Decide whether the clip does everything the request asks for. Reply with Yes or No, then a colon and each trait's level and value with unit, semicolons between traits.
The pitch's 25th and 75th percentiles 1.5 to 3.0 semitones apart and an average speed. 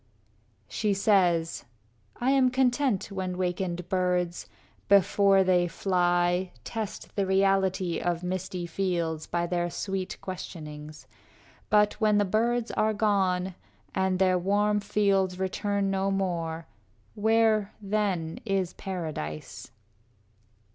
No: narrow, 2.5 semitones; slow, 115 wpm